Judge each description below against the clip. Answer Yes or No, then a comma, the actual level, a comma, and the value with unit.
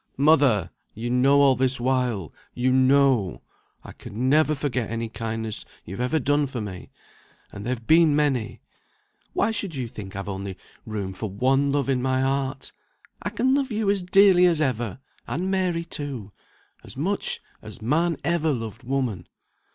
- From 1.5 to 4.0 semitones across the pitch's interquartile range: No, average, 5.2 semitones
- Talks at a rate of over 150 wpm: Yes, average, 165 wpm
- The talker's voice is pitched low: Yes, low, 130 Hz